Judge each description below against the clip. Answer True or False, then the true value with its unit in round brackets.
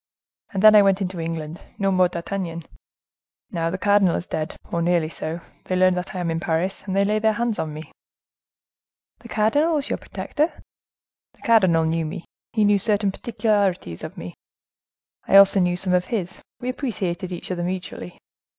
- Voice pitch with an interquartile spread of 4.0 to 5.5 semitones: False (3.5 semitones)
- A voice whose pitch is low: False (185 Hz)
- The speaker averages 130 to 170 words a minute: False (180 wpm)